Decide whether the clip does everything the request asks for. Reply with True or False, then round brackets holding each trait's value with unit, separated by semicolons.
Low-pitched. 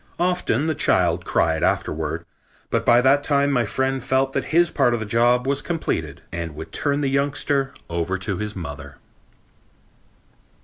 True (130 Hz)